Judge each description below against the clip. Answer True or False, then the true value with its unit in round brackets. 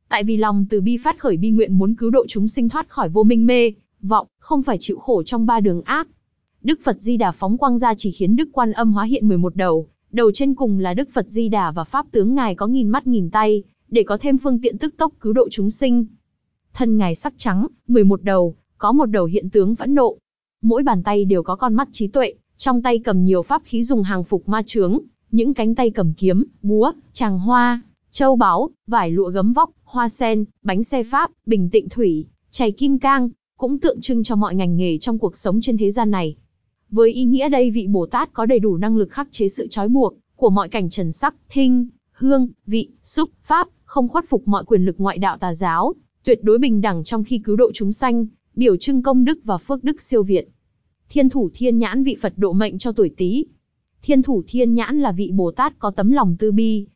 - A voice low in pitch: False (225 Hz)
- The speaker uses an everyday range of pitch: True (4.2 semitones)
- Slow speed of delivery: False (235 wpm)